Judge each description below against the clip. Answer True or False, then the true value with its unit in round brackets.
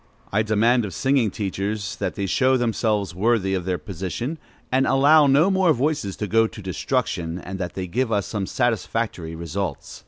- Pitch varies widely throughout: False (5.0 semitones)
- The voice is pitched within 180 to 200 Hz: False (105 Hz)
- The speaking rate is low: False (180 wpm)